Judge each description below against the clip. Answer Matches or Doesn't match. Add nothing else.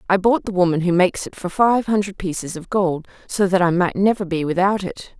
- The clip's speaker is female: Matches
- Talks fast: Matches